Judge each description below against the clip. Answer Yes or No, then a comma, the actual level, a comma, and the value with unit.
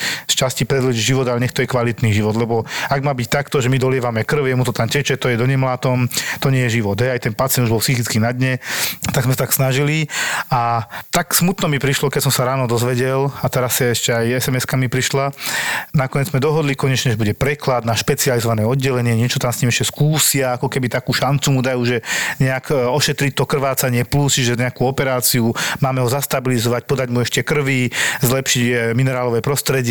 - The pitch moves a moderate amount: No, narrow, 2.1 semitones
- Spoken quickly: Yes, fast, 210 wpm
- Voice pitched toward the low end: Yes, low, 130 Hz